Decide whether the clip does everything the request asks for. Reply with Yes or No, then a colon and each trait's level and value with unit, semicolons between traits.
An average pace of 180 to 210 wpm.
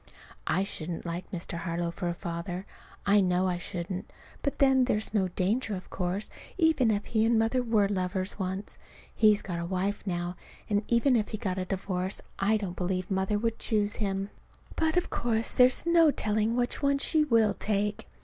Yes: average, 190 wpm